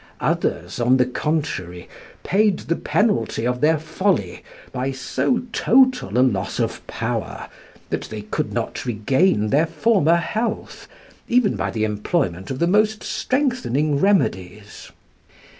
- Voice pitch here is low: No, medium, 145 Hz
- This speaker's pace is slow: Yes, slow, 130 wpm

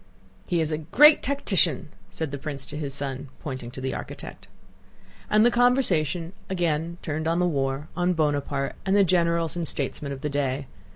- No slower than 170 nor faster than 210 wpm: Yes, average, 180 wpm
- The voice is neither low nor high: Yes, medium, 155 Hz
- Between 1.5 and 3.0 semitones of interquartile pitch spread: No, average, 3.9 semitones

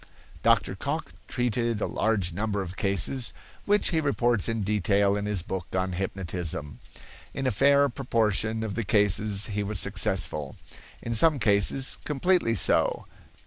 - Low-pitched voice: Yes, low, 105 Hz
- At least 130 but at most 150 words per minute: Yes, average, 145 wpm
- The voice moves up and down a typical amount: Yes, average, 3.9 semitones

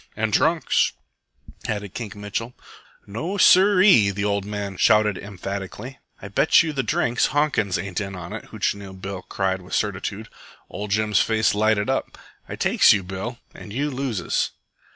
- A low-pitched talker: Yes, low, 105 Hz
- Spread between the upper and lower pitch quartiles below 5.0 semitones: Yes, average, 3.2 semitones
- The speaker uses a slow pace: No, average, 160 wpm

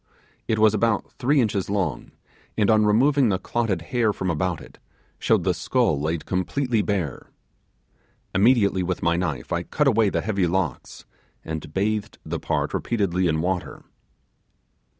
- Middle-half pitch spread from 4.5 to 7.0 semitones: No, average, 4.1 semitones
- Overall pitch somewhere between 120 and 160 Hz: No, low, 100 Hz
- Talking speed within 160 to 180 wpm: No, average, 150 wpm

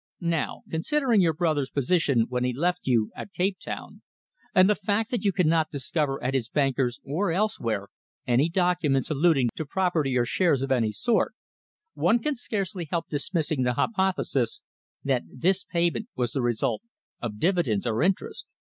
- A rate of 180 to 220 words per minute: No, average, 165 wpm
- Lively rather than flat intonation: Yes, wide, 6.2 semitones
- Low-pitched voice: No, medium, 160 Hz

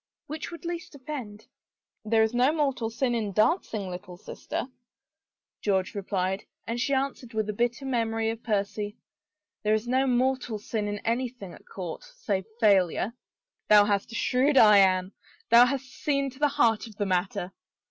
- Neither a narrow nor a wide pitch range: Yes, average, 4.3 semitones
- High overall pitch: Yes, high, 225 Hz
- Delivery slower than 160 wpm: No, average, 180 wpm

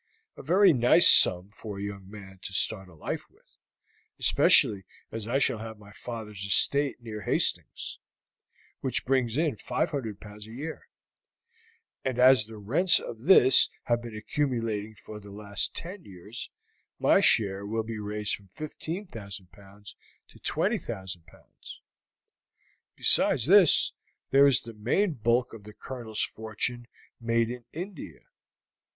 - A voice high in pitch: No, low, 110 Hz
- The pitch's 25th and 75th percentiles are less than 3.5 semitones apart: No, average, 4.0 semitones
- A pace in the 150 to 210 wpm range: No, average, 140 wpm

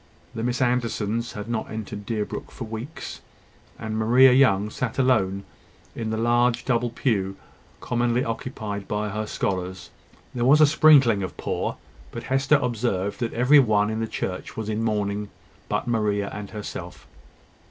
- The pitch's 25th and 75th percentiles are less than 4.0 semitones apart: Yes, average, 3.0 semitones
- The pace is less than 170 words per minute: Yes, average, 155 wpm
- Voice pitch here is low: Yes, low, 110 Hz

